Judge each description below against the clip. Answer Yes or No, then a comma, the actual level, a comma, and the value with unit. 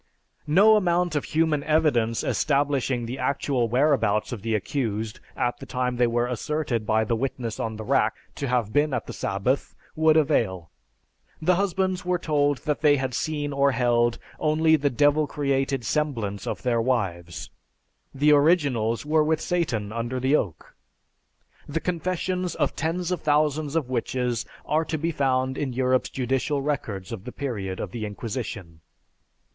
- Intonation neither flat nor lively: Yes, average, 4.7 semitones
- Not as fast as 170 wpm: Yes, average, 160 wpm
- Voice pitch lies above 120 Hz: Yes, low, 135 Hz